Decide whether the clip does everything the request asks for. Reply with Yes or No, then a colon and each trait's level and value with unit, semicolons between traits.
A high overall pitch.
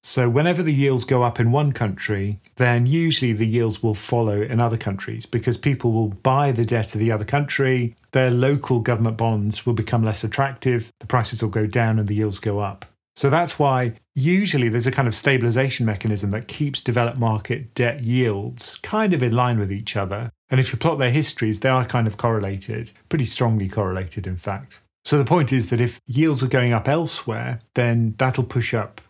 No: low, 120 Hz